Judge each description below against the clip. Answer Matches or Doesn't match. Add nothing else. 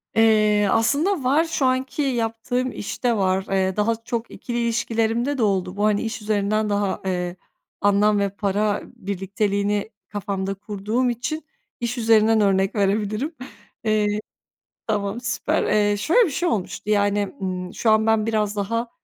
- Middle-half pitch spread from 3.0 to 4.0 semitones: Doesn't match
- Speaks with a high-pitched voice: Matches